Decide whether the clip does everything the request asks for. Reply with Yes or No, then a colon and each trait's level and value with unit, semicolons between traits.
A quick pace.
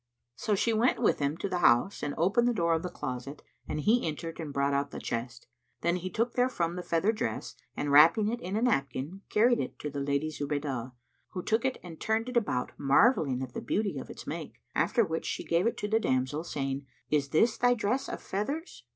Yes: fast, 225 wpm